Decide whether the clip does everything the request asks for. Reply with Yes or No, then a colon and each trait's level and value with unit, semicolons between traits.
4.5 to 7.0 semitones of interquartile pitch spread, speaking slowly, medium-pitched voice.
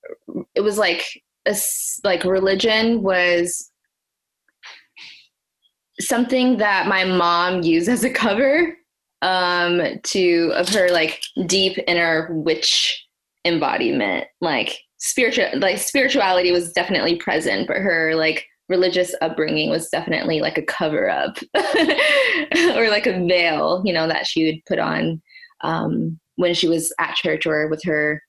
Yes: average, 5.3 semitones; slow, 130 wpm; medium, 180 Hz